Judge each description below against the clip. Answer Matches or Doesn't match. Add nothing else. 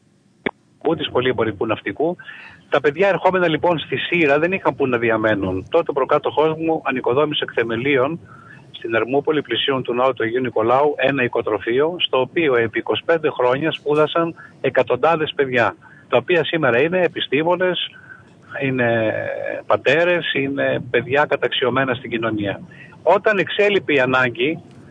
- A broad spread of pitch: Matches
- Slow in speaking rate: Doesn't match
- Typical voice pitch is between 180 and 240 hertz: Doesn't match